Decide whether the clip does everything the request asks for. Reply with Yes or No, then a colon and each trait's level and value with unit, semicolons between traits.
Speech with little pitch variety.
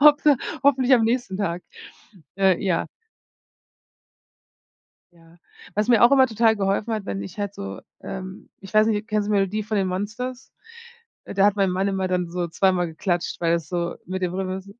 No: average, 3.2 semitones